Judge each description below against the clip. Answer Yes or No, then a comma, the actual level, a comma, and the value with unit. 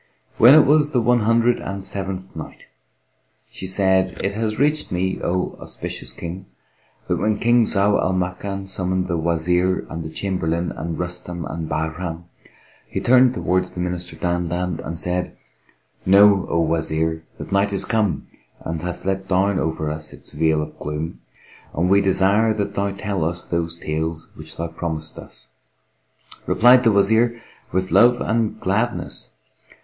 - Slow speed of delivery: No, average, 160 wpm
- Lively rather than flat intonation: No, average, 3.3 semitones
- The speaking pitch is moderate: No, very low, 95 Hz